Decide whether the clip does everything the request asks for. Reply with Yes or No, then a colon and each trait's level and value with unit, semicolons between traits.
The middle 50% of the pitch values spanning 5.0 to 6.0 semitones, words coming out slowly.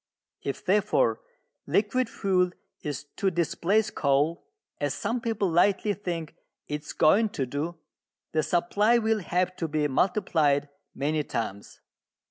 Yes: wide, 5.6 semitones; slow, 130 wpm